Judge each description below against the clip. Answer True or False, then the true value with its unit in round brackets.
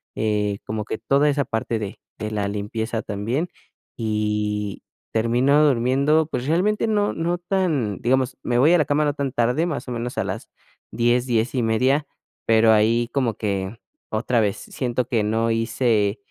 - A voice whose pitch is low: True (120 Hz)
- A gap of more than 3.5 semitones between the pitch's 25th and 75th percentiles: True (4.3 semitones)